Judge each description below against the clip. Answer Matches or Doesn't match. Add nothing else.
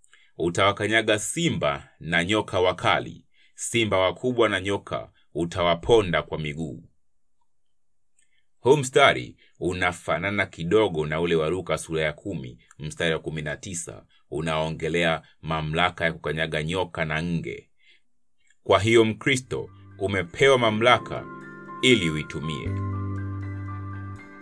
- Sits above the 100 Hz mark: Doesn't match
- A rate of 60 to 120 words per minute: Matches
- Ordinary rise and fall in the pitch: Matches